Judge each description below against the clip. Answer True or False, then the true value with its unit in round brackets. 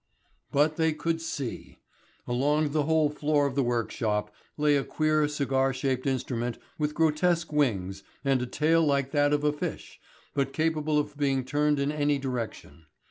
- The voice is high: False (145 Hz)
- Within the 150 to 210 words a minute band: True (165 wpm)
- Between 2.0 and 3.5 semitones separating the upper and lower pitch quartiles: True (2.6 semitones)